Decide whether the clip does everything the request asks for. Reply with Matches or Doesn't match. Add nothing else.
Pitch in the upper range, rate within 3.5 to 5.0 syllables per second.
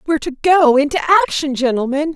Doesn't match